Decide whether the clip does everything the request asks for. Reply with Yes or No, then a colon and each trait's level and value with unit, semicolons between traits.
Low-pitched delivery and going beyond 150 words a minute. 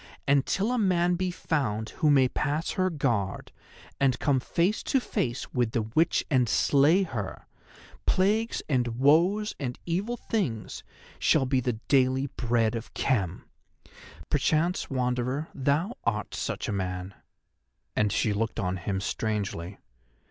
No: low, 130 Hz; average, 140 wpm